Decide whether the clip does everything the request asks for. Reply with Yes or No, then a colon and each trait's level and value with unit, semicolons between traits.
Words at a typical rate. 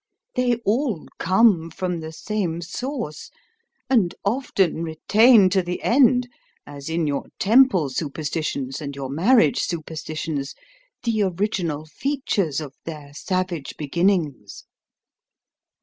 No: slow, 110 wpm